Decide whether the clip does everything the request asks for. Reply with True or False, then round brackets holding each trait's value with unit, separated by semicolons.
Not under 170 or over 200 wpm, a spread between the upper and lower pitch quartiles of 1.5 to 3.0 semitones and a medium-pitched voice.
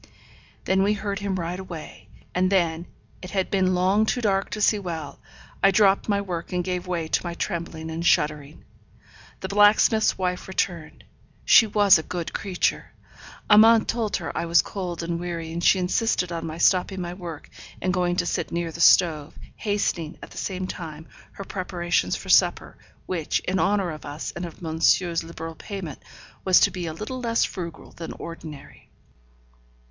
True (180 wpm; 2.7 semitones; 180 Hz)